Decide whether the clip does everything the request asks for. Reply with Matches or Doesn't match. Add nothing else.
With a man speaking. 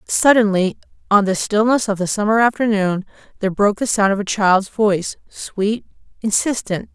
Doesn't match